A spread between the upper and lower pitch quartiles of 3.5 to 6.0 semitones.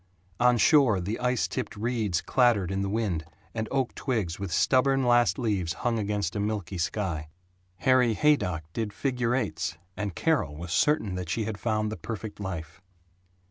Yes: average, 4.9 semitones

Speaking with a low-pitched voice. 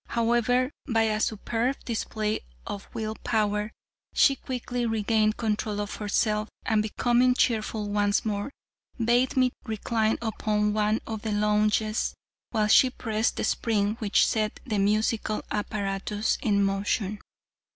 No: high, 215 Hz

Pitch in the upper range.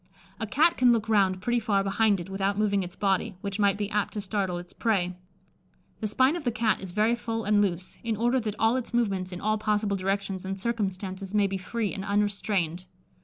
Yes: high, 205 Hz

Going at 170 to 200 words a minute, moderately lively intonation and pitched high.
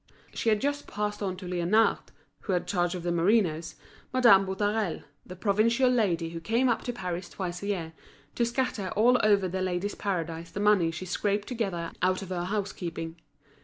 Yes: average, 190 wpm; average, 3.5 semitones; high, 195 Hz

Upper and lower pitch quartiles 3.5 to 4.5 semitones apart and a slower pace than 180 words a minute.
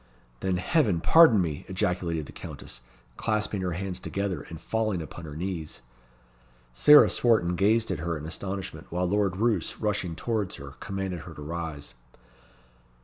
Yes: average, 4.0 semitones; average, 150 wpm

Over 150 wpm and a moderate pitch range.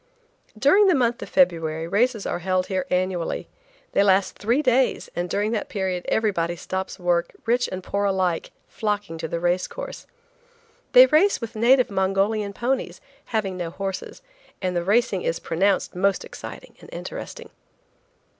Yes: average, 160 wpm; average, 4.4 semitones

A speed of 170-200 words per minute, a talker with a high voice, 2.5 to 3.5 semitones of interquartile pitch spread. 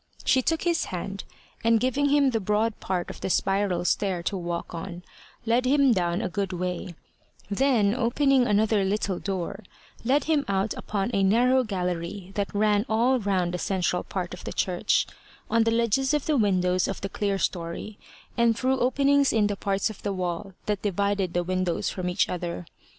No: average, 185 wpm; high, 200 Hz; average, 4.3 semitones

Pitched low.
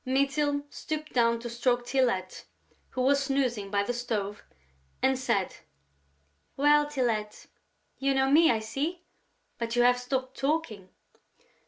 No: very high, 255 Hz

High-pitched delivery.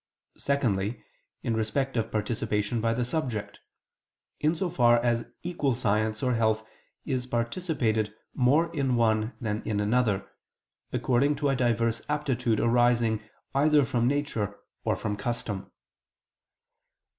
No: low, 120 Hz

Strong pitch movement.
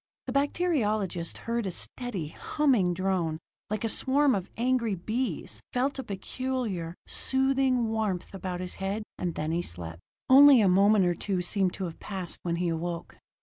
Yes: wide, 6.1 semitones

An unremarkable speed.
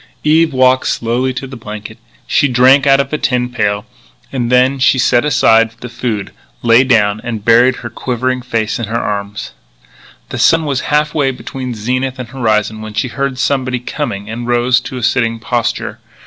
Yes: average, 180 wpm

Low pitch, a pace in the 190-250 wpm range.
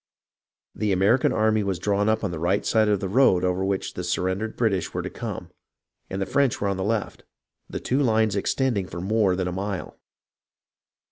Yes: low, 100 Hz; fast, 205 wpm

